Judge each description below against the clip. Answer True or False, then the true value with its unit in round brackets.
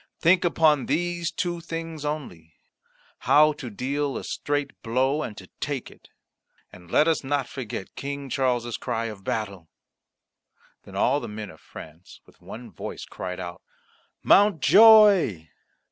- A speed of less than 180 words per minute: True (145 wpm)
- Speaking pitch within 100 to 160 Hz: True (135 Hz)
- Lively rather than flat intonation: True (6.5 semitones)